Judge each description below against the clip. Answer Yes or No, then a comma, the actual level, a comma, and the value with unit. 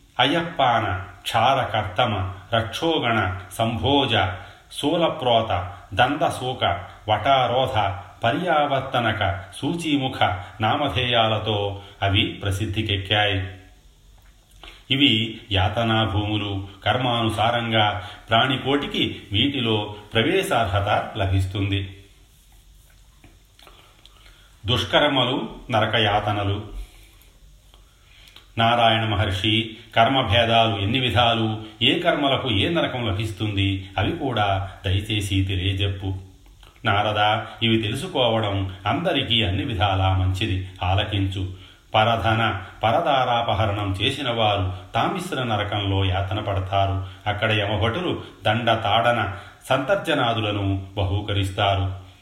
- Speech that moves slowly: Yes, slow, 65 wpm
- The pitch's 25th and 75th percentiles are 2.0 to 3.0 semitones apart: Yes, narrow, 2.6 semitones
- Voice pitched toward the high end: No, low, 105 Hz